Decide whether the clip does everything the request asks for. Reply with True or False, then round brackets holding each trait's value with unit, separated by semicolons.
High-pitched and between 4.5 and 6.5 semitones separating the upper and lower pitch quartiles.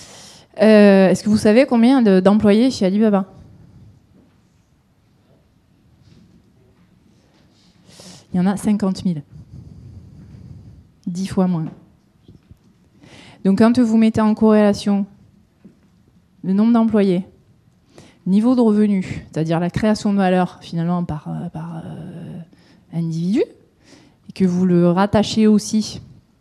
False (195 Hz; 3.7 semitones)